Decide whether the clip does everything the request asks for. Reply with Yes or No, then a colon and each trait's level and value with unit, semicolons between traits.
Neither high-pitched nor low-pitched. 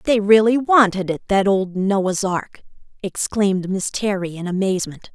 No: high, 195 Hz